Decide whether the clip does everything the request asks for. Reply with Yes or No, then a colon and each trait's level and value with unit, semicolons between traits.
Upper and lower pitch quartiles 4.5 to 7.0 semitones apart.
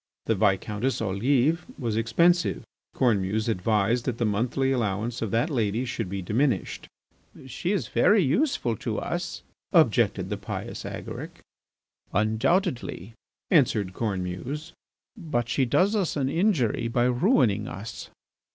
Yes: average, 5.0 semitones